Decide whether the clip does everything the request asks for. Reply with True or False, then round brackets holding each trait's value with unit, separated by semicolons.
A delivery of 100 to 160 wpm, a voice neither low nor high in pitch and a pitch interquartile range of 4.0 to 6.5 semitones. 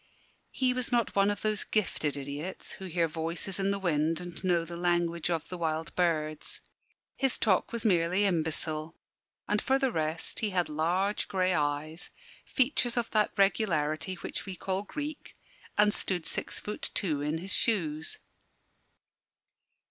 True (155 wpm; 180 Hz; 4.4 semitones)